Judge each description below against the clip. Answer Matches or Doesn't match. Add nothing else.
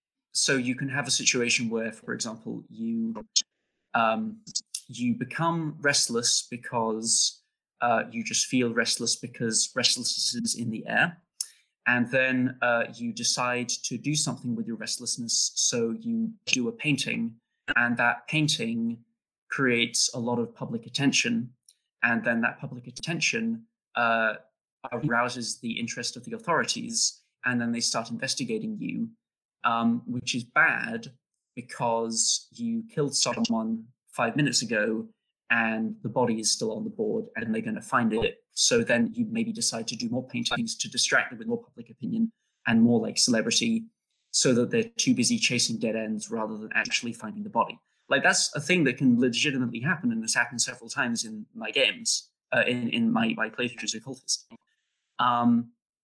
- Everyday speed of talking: Matches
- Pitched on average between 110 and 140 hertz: Matches